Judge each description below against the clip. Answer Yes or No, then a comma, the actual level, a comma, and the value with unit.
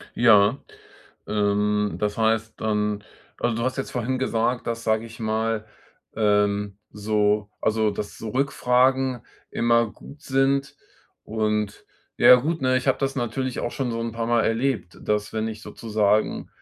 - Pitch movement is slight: No, average, 3.0 semitones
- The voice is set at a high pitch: No, low, 115 Hz